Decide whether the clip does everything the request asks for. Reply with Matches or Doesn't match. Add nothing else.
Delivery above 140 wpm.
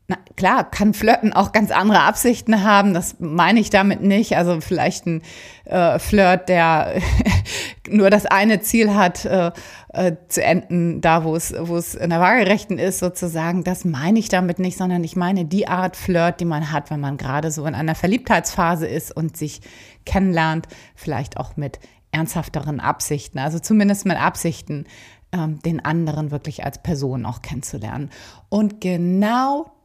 Matches